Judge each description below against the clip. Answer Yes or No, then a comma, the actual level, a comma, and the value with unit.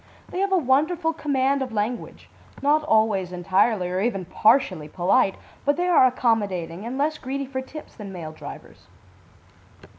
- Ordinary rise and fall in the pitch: No, wide, 6.6 semitones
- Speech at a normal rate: Yes, average, 155 wpm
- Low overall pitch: No, high, 245 Hz